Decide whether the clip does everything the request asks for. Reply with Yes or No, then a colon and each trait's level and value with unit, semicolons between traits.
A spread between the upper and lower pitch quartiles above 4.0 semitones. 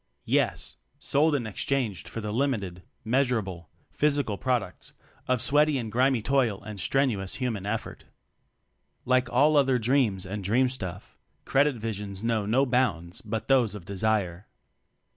Yes: average, 4.6 semitones